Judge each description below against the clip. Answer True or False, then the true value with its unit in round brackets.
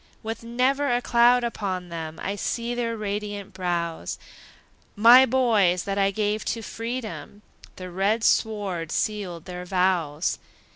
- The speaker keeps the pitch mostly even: False (4.3 semitones)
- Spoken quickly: False (135 wpm)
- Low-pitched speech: False (205 Hz)